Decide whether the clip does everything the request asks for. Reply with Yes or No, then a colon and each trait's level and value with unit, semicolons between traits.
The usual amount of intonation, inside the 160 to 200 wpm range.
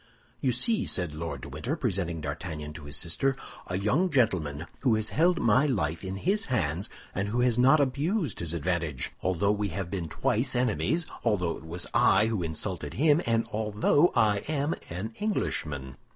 No: wide, 7.7 semitones; average, 180 wpm